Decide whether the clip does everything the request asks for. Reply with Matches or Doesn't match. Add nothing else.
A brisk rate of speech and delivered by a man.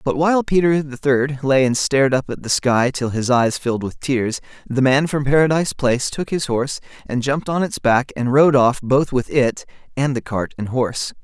Matches